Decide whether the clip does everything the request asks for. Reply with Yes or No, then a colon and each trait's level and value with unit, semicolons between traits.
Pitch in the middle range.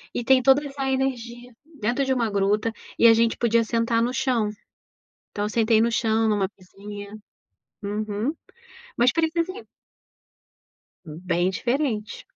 No: high, 230 Hz